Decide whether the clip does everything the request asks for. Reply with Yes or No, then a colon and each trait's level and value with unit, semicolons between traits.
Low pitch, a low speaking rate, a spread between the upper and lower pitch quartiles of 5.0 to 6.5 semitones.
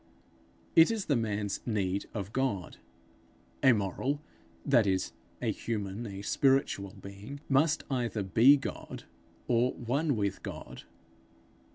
Yes: low, 115 Hz; slow, 125 wpm; wide, 5.4 semitones